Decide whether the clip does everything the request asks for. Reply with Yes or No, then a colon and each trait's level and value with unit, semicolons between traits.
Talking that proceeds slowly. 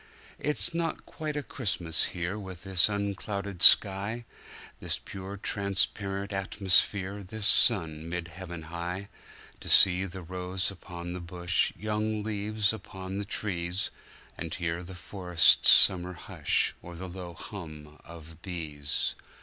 Yes: slow, 125 wpm